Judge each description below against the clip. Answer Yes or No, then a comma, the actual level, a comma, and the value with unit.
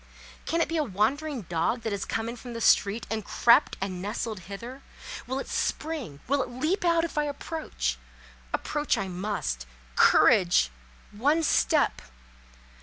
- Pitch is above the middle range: Yes, high, 230 Hz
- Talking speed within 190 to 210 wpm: No, average, 160 wpm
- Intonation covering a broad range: Yes, wide, 7.1 semitones